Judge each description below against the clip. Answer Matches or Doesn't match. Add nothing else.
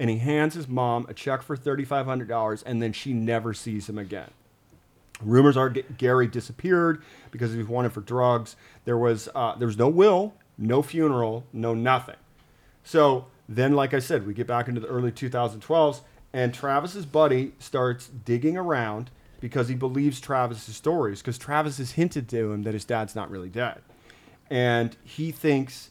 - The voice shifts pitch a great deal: Doesn't match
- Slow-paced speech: Doesn't match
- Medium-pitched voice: Doesn't match